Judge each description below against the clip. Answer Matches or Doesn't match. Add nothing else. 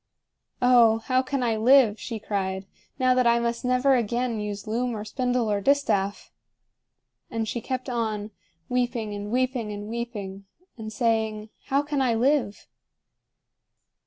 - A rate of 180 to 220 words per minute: Doesn't match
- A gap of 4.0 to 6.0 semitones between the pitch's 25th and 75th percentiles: Doesn't match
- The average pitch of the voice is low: Doesn't match